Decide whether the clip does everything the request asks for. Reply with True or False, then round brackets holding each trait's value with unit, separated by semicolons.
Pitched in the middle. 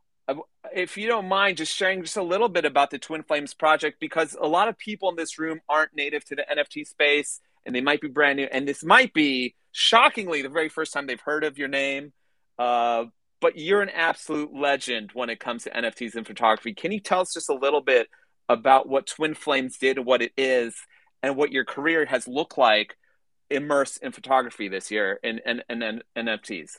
True (145 Hz)